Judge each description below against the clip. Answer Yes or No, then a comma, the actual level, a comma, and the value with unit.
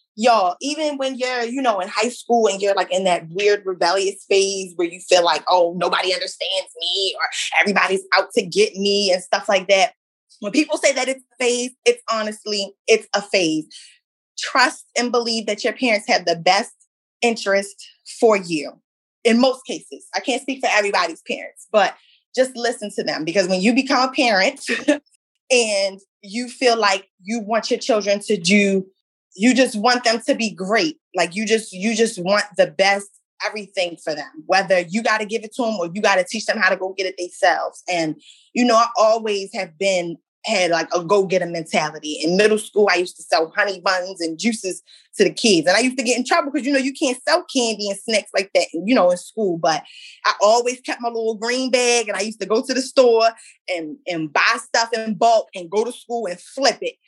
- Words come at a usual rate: No, fast, 215 wpm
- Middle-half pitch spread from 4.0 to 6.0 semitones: Yes, average, 4.4 semitones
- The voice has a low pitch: No, high, 215 Hz